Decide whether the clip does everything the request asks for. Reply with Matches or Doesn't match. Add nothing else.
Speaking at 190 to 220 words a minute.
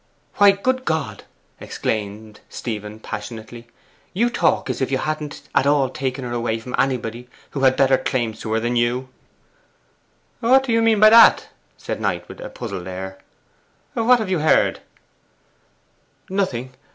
Doesn't match